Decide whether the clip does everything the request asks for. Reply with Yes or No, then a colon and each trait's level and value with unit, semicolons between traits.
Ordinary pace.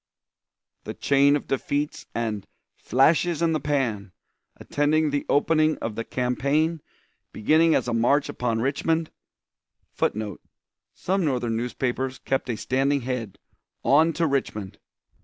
No: slow, 130 wpm